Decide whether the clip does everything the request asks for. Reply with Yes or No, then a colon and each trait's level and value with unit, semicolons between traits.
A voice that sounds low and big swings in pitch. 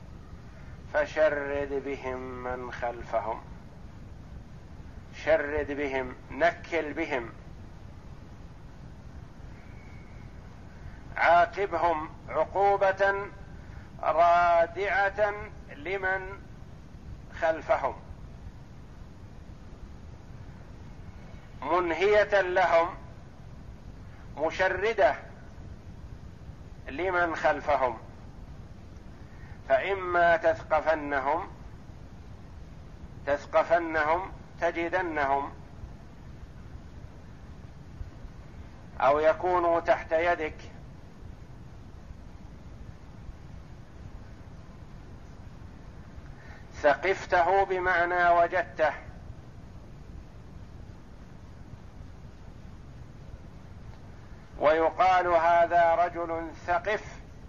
No: medium, 155 Hz; wide, 6.8 semitones